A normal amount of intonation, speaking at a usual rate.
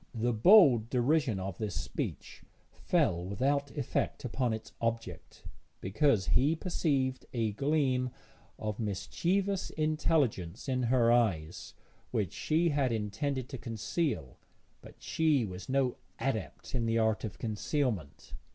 No: average, 4.8 semitones; slow, 125 wpm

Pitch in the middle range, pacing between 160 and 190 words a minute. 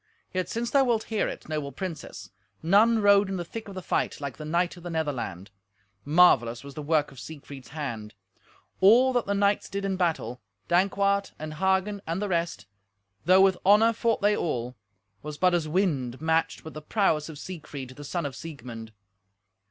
Yes: medium, 165 Hz; average, 185 wpm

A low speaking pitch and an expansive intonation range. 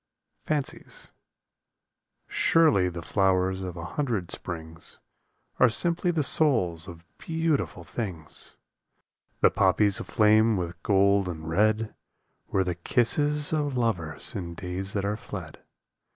Yes: low, 100 Hz; wide, 5.7 semitones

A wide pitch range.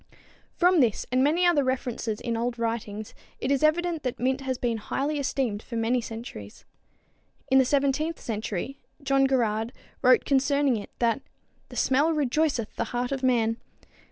No: average, 3.4 semitones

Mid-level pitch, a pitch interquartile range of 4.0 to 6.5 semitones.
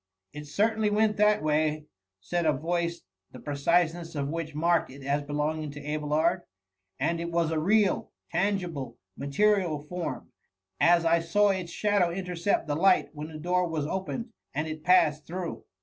No: medium, 165 Hz; average, 3.3 semitones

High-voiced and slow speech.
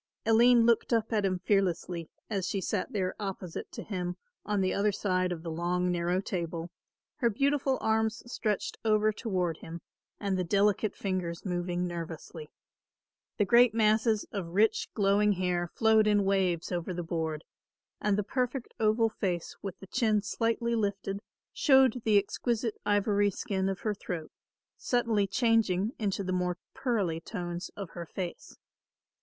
No: high, 200 Hz; average, 155 wpm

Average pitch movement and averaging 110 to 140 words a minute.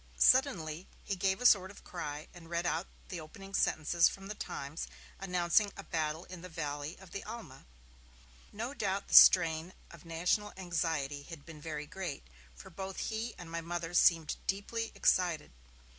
No: average, 3.4 semitones; average, 170 wpm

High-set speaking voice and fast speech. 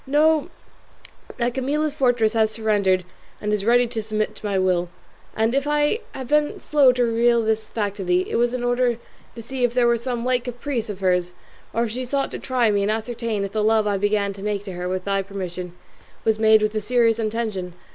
Yes: high, 225 Hz; fast, 225 wpm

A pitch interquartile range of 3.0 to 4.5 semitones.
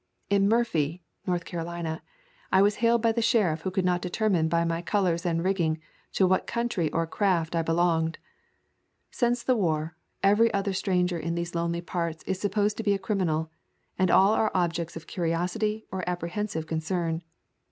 Yes: average, 3.4 semitones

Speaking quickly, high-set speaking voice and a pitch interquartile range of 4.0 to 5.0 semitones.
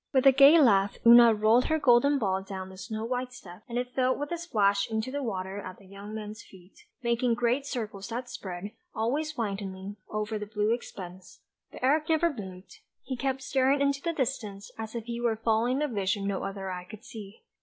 Yes: fast, 210 wpm; high, 225 Hz; average, 4.4 semitones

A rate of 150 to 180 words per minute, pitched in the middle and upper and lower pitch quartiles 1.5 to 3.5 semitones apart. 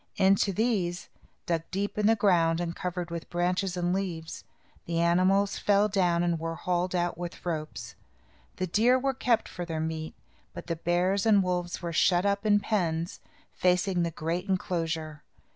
Yes: average, 170 wpm; medium, 180 Hz; narrow, 2.6 semitones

